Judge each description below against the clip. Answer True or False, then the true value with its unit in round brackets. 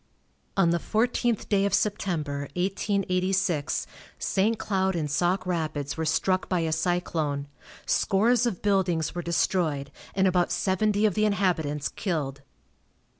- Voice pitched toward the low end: False (180 Hz)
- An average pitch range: True (3.7 semitones)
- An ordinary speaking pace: False (130 wpm)